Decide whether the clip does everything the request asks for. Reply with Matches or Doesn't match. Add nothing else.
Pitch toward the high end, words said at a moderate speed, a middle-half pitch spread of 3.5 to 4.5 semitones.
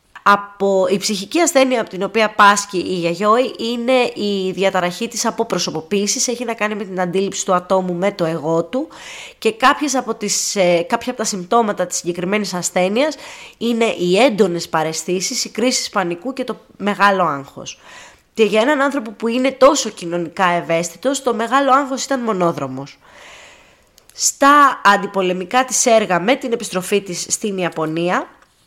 Doesn't match